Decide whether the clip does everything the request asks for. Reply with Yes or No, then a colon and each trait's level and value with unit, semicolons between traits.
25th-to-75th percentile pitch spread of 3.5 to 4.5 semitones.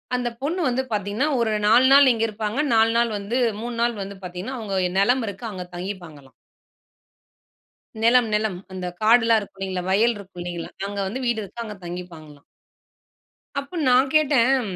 Yes: average, 4.2 semitones